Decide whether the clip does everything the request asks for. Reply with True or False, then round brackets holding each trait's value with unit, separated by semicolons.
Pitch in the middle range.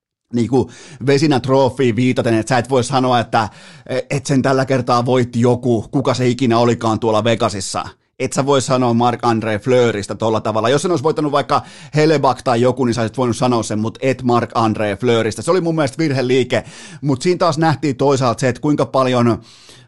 False (125 Hz)